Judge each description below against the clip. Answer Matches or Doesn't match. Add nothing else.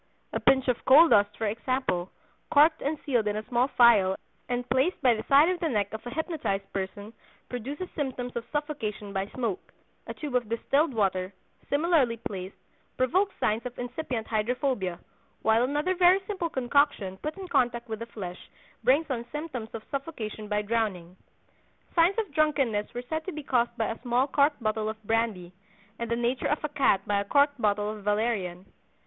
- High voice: Matches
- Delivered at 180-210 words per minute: Matches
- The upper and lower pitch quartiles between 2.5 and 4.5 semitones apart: Doesn't match